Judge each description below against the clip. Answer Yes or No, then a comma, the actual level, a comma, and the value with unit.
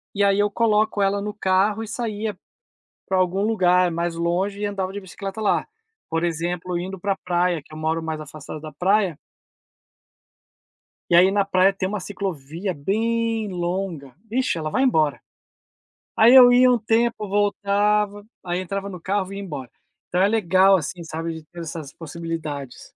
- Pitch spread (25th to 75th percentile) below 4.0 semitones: Yes, average, 3.4 semitones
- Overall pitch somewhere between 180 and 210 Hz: Yes, high, 190 Hz